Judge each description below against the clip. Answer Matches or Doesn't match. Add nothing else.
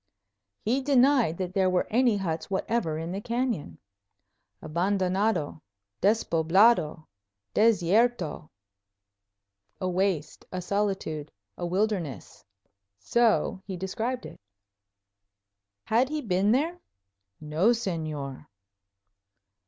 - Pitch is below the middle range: Doesn't match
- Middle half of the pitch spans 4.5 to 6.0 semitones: Matches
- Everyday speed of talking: Doesn't match